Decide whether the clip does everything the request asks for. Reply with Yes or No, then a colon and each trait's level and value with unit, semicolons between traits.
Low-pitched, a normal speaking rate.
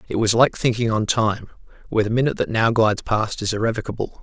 No: low, 110 Hz; fast, 215 wpm